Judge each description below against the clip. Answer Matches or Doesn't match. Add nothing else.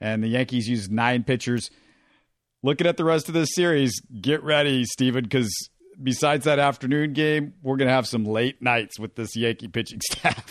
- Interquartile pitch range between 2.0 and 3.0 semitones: Doesn't match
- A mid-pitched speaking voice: Doesn't match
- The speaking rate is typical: Matches